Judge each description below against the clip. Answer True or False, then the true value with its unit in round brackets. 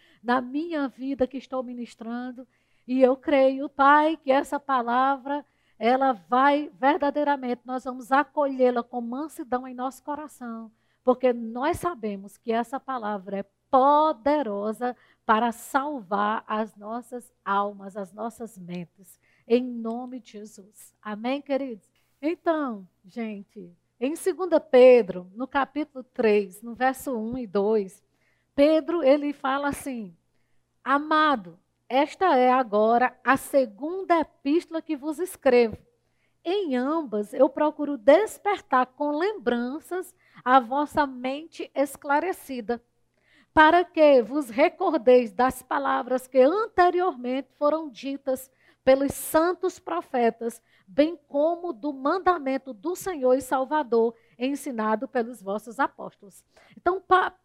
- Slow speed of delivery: True (115 wpm)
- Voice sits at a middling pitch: False (265 Hz)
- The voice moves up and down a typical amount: True (3.8 semitones)